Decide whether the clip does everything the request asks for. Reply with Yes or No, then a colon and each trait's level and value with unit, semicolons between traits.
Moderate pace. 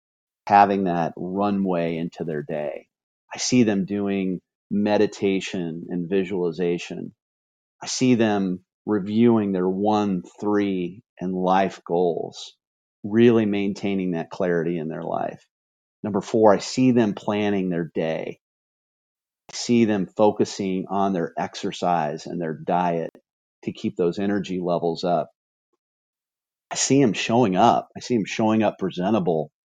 No: slow, 130 wpm